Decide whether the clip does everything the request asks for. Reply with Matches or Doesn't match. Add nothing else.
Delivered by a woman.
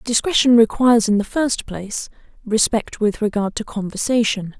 Matches